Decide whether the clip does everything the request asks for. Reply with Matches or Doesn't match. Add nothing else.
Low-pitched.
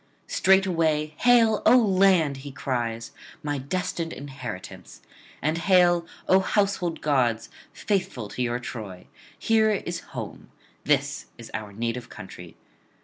Doesn't match